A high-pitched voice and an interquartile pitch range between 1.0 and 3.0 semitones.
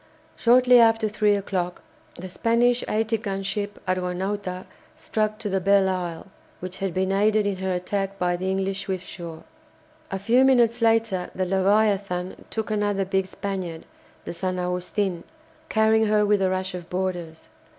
Yes: high, 195 Hz; narrow, 2.6 semitones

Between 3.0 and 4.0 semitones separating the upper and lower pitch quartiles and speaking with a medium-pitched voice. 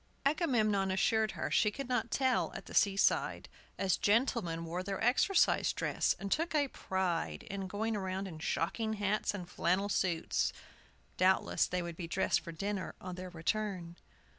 No: average, 3.4 semitones; high, 195 Hz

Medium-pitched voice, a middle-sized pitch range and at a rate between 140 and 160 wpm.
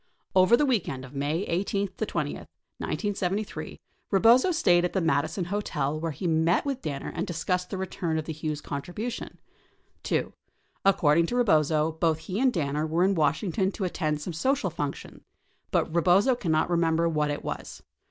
No: medium, 170 Hz; average, 4.1 semitones; average, 170 wpm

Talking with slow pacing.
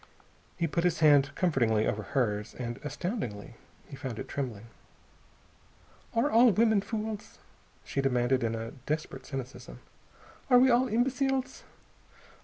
Yes: slow, 130 wpm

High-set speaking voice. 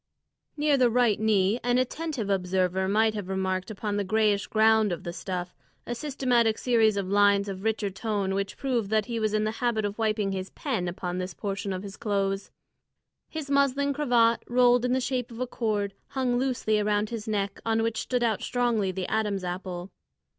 Yes: high, 215 Hz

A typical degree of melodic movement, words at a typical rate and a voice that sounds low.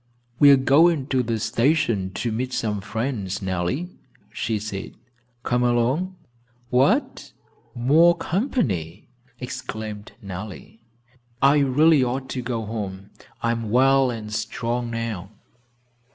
No: average, 4.1 semitones; slow, 120 wpm; low, 120 Hz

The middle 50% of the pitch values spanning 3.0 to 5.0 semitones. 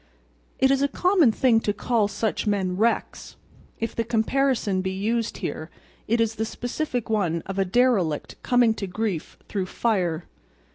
Yes: average, 4.0 semitones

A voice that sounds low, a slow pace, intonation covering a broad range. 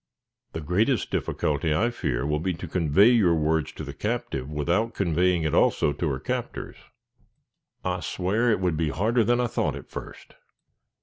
No: very low, 90 Hz; average, 175 wpm; wide, 6.2 semitones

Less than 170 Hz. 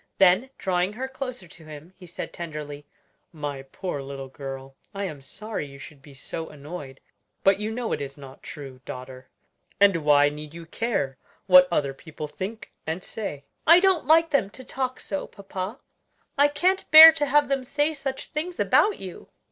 No: medium, 180 Hz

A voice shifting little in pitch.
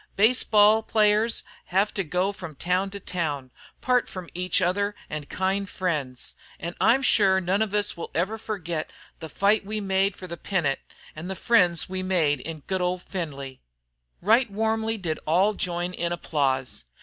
No: average, 3.5 semitones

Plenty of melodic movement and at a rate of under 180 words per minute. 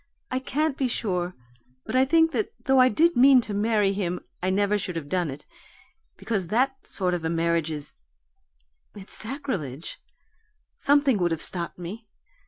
Yes: wide, 7.0 semitones; average, 170 wpm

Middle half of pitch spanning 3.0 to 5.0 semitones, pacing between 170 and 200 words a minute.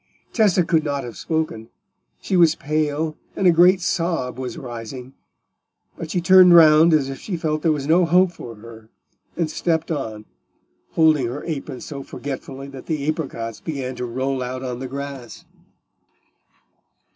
No: average, 4.2 semitones; average, 160 wpm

